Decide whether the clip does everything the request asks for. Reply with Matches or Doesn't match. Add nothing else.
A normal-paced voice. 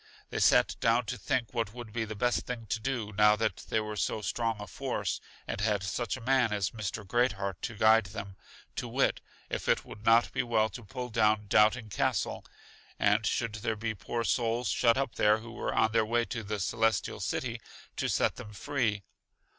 Doesn't match